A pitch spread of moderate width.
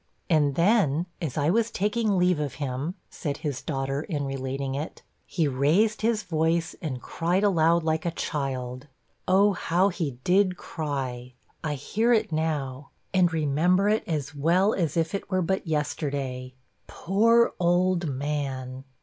Yes: average, 4.8 semitones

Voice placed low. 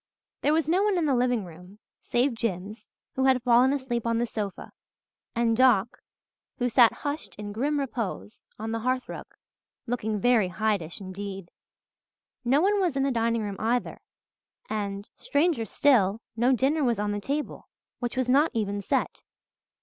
No: high, 235 Hz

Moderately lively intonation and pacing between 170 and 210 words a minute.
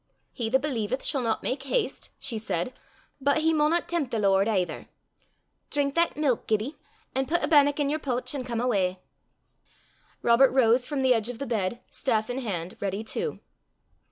Yes: average, 4.3 semitones; average, 185 wpm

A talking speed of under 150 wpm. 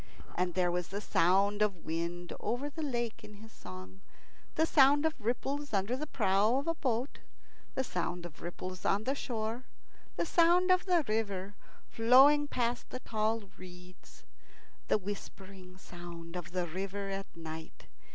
No: average, 160 wpm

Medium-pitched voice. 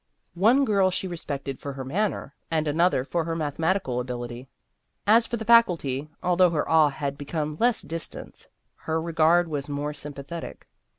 Yes: medium, 160 Hz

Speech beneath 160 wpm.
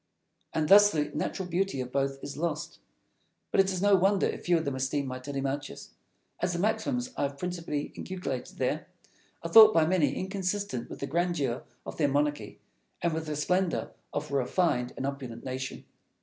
No: average, 185 wpm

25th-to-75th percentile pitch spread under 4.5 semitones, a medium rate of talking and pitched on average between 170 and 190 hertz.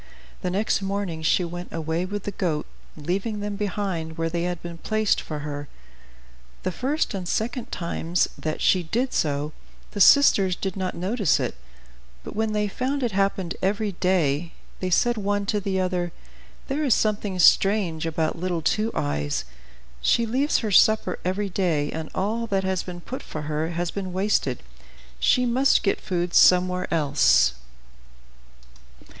Yes: average, 3.9 semitones; average, 160 wpm; medium, 185 Hz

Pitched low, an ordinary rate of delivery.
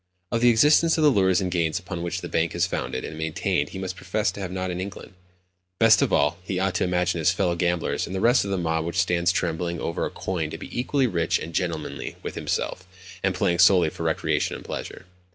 No: very low, 90 Hz; fast, 240 wpm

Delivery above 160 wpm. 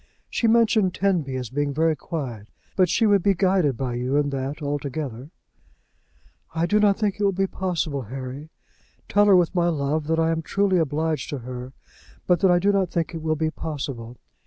Yes: average, 200 wpm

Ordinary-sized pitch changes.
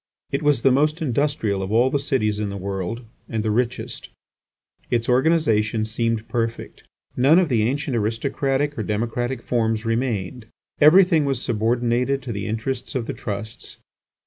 Yes: average, 3.9 semitones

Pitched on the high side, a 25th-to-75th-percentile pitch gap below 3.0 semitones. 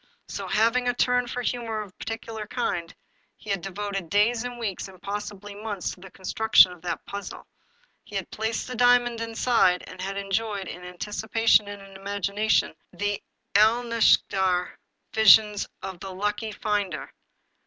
Yes: high, 205 Hz; narrow, 2.6 semitones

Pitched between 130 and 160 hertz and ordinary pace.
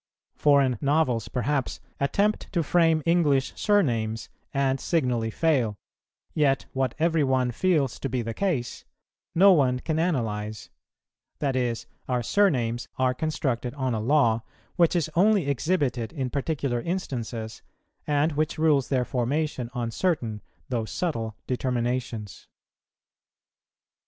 No: low, 135 Hz; slow, 125 wpm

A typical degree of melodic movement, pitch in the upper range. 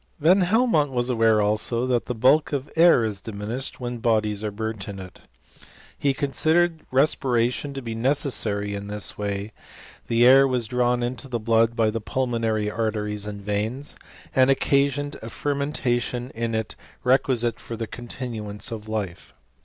No: average, 3.7 semitones; low, 120 Hz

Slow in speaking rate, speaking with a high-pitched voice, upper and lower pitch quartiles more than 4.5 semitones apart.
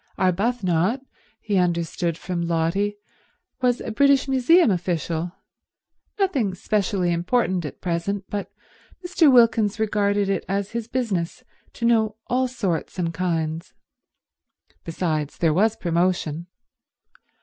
Yes: slow, 110 wpm; high, 195 Hz; average, 5.1 semitones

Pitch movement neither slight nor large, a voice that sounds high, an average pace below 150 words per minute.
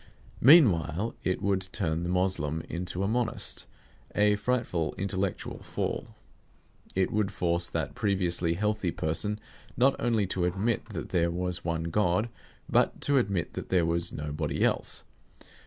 No: average, 3.6 semitones; very low, 95 Hz; average, 140 wpm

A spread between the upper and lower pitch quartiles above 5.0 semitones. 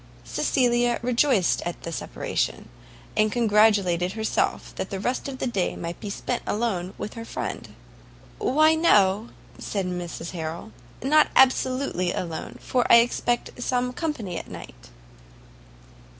Yes: wide, 5.4 semitones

